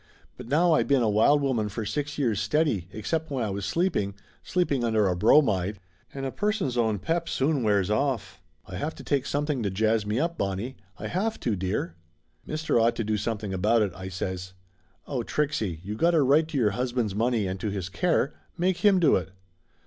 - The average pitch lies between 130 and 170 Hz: No, low, 115 Hz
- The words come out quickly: Yes, fast, 215 wpm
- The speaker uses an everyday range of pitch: No, wide, 6.6 semitones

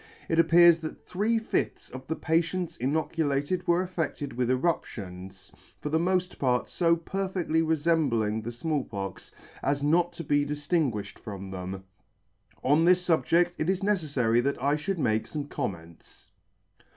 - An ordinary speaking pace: Yes, average, 150 wpm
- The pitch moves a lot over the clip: Yes, wide, 5.7 semitones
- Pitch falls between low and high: Yes, medium, 150 Hz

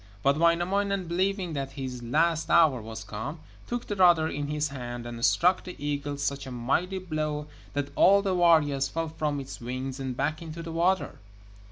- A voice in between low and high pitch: Yes, medium, 150 Hz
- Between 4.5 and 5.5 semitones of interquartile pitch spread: No, average, 4.1 semitones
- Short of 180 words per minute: No, average, 185 wpm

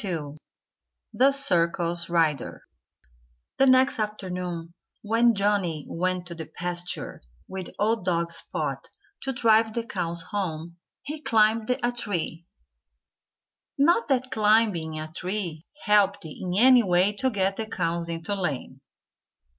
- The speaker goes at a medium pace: No, slow, 130 wpm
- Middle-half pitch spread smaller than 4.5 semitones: No, average, 4.8 semitones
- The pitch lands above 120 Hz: Yes, high, 190 Hz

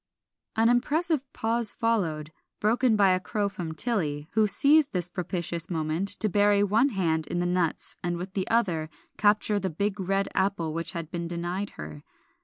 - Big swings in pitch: No, average, 4.1 semitones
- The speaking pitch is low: No, high, 190 Hz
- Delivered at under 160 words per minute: No, average, 175 wpm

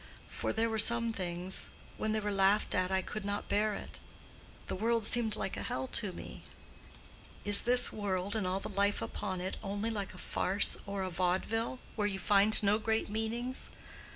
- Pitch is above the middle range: Yes, high, 205 Hz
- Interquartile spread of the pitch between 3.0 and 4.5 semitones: No, narrow, 2.5 semitones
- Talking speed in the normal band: Yes, average, 185 wpm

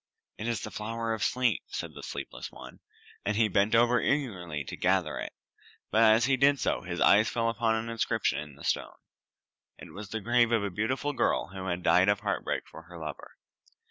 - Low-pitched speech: Yes, low, 110 Hz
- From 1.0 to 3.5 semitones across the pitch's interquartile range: No, average, 3.9 semitones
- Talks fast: Yes, fast, 210 wpm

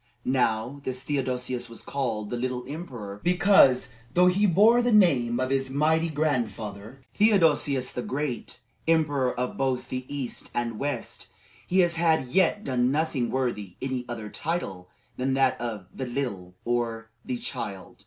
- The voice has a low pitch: Yes, low, 130 Hz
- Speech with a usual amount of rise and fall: Yes, average, 4.3 semitones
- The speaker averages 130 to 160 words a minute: Yes, average, 150 wpm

